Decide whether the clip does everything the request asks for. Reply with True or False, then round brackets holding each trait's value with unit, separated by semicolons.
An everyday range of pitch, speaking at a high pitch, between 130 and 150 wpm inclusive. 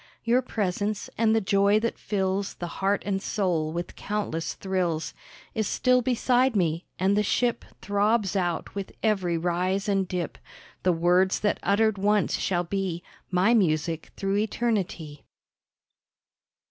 True (3.1 semitones; 195 Hz; 140 wpm)